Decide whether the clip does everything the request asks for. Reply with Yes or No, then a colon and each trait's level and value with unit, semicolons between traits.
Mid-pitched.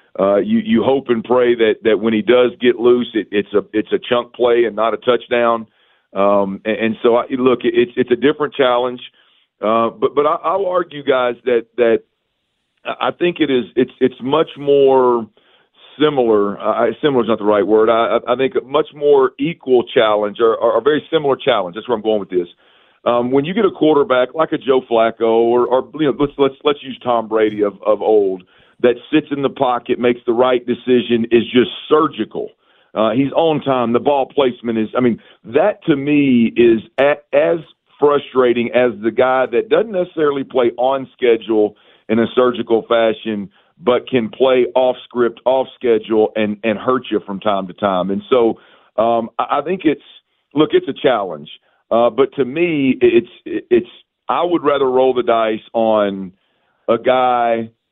No: low, 125 Hz